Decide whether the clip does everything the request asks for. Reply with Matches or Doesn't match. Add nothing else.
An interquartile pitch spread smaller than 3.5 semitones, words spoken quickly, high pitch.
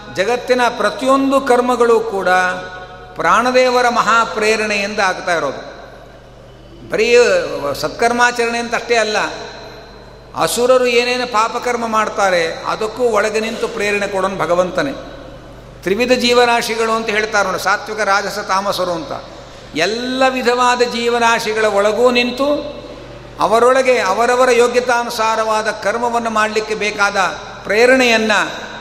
Doesn't match